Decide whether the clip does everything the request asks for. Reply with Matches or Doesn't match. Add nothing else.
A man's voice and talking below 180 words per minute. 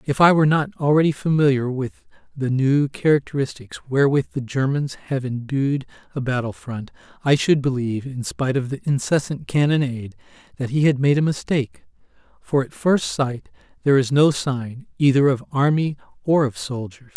Matches